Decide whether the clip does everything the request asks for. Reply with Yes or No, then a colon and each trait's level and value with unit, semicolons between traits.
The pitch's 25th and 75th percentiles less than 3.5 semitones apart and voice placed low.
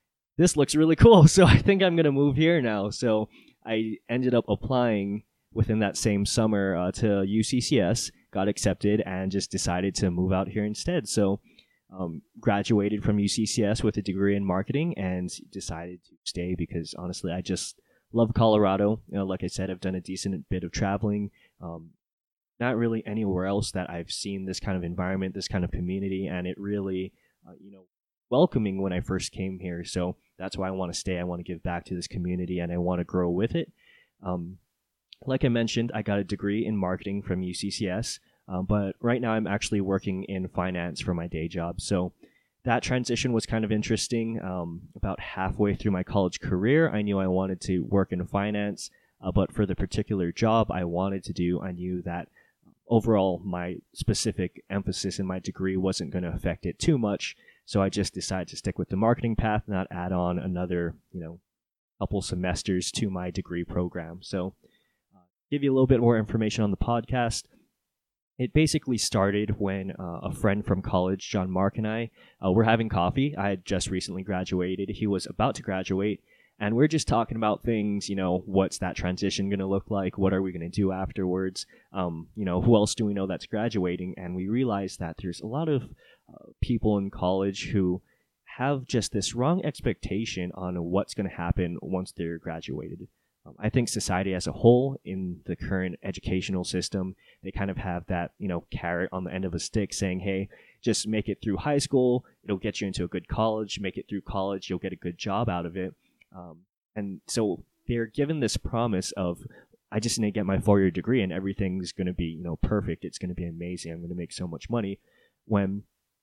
Yes: average, 3.0 semitones; very low, 95 Hz